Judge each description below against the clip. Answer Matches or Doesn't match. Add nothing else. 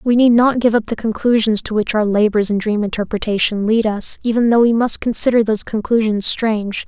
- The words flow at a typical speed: Doesn't match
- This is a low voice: Doesn't match